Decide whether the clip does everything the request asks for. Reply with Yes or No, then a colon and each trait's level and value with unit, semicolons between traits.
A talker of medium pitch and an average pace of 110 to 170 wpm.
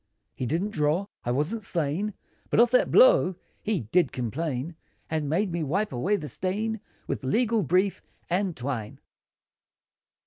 Yes: medium, 175 Hz; average, 145 wpm